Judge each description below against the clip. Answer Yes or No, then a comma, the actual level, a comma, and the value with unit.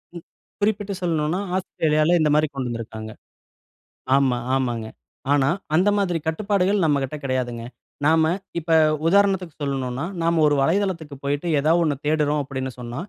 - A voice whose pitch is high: No, medium, 155 Hz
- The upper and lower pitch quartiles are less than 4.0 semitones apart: No, average, 4.3 semitones